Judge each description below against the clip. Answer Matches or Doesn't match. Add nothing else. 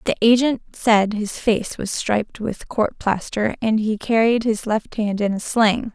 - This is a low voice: Doesn't match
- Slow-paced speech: Doesn't match